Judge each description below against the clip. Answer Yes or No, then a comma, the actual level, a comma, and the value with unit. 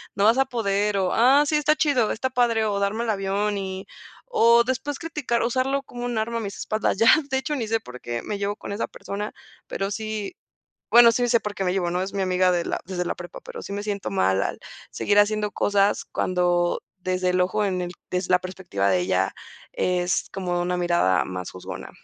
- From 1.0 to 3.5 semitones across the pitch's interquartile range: No, average, 4.2 semitones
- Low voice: No, high, 200 Hz